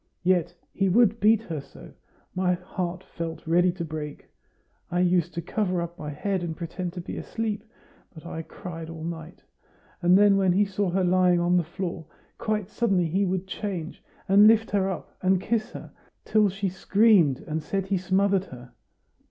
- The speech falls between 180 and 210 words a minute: Yes, average, 185 wpm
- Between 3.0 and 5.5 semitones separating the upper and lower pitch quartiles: No, narrow, 2.6 semitones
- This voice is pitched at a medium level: Yes, medium, 180 Hz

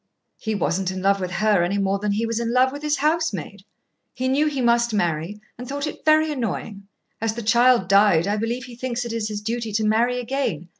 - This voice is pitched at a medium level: No, high, 230 Hz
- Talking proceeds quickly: Yes, fast, 220 wpm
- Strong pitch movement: No, average, 4.0 semitones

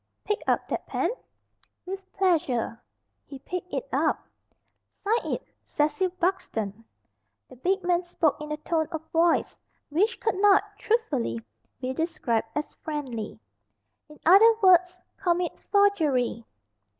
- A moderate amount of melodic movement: No, wide, 5.7 semitones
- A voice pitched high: Yes, very high, 335 Hz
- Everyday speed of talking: No, slow, 125 wpm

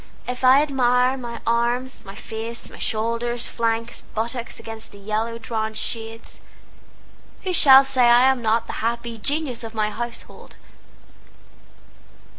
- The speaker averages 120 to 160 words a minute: Yes, slow, 135 wpm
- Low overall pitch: No, high, 235 Hz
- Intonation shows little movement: Yes, narrow, 1.9 semitones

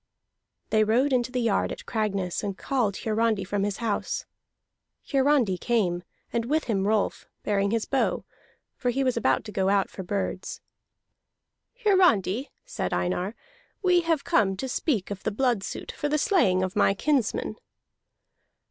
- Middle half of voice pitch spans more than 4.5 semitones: Yes, average, 5.1 semitones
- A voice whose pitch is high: Yes, high, 220 Hz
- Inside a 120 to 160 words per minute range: Yes, average, 155 wpm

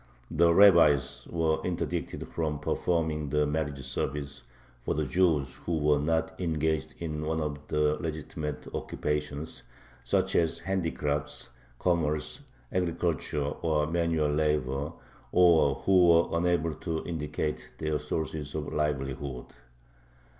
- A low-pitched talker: Yes, very low, 75 Hz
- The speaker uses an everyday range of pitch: No, narrow, 2.0 semitones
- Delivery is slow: Yes, slow, 120 wpm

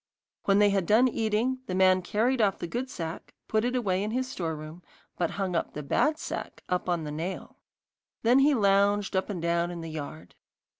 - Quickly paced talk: Yes, fast, 210 wpm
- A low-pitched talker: No, high, 195 Hz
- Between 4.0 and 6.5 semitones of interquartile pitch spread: Yes, average, 4.8 semitones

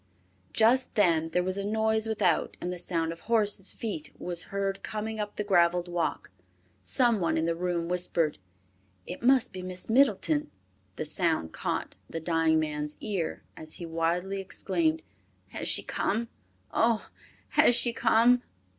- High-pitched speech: No, medium, 180 Hz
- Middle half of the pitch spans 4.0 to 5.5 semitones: Yes, average, 4.7 semitones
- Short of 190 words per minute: Yes, average, 155 wpm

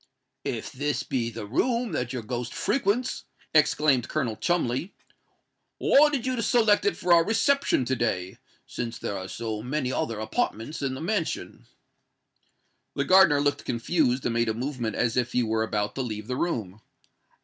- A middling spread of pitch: No, wide, 7.1 semitones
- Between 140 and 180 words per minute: Yes, average, 170 wpm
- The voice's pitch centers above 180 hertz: No, low, 130 Hz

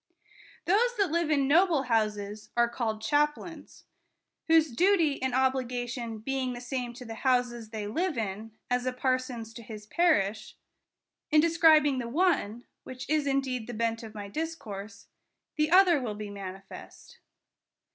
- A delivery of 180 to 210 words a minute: No, average, 165 wpm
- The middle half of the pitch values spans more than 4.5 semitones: Yes, wide, 5.5 semitones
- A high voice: Yes, very high, 250 Hz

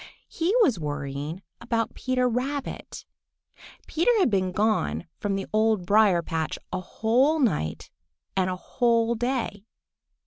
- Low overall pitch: No, high, 215 Hz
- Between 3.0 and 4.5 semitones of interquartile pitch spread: No, wide, 5.4 semitones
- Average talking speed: No, slow, 130 wpm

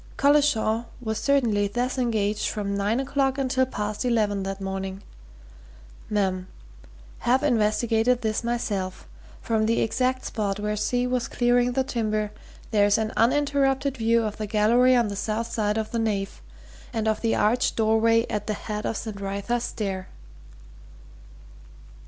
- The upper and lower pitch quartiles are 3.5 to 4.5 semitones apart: No, average, 2.9 semitones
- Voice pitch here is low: No, high, 220 Hz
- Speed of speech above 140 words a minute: Yes, average, 150 wpm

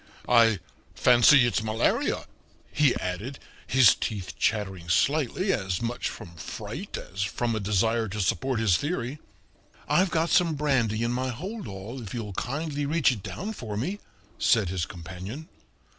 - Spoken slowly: No, average, 150 wpm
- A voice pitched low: Yes, low, 115 Hz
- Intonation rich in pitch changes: Yes, wide, 5.9 semitones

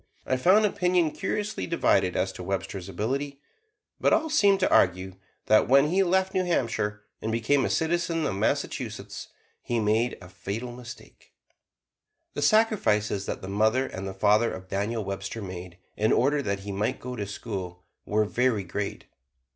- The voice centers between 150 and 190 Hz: No, low, 110 Hz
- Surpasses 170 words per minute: No, average, 165 wpm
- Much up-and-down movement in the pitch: Yes, wide, 7.1 semitones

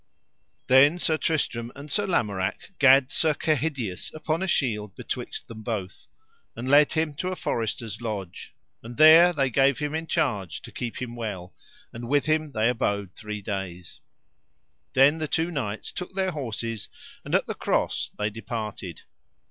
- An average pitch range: No, wide, 6.4 semitones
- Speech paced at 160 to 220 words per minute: Yes, average, 165 wpm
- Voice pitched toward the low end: Yes, low, 125 Hz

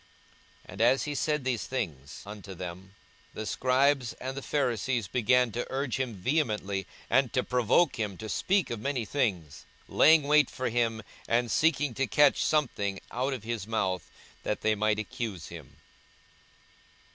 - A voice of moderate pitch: No, low, 120 Hz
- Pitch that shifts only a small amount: No, average, 4.5 semitones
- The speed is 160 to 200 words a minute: Yes, average, 165 wpm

